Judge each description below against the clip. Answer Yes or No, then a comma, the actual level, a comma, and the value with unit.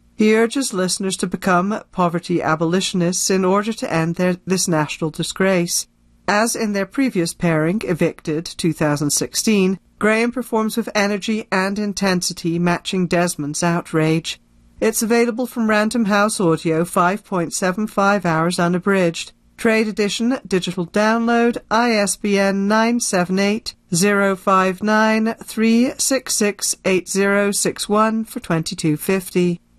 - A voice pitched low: No, high, 195 Hz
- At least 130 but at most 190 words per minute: Yes, slow, 135 wpm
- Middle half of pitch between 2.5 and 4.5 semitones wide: Yes, average, 3.8 semitones